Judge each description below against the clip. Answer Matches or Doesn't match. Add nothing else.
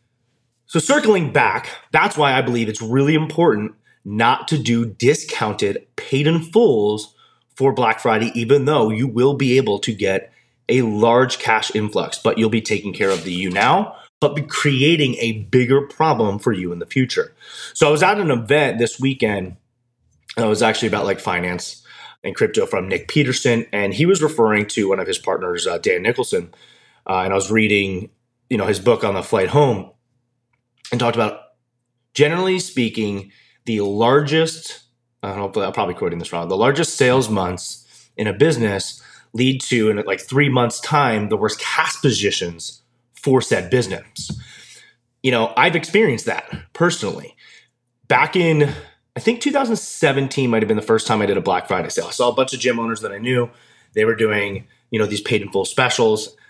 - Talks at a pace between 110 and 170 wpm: Doesn't match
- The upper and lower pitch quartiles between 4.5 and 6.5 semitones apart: Matches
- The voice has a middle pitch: Doesn't match